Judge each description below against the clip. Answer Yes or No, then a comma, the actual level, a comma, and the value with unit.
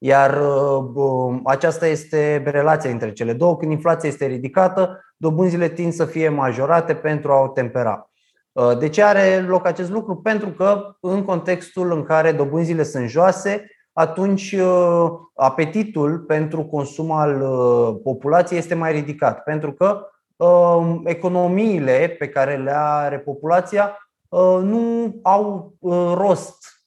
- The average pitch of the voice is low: No, medium, 165 Hz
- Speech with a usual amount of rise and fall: Yes, average, 4.2 semitones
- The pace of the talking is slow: No, average, 125 wpm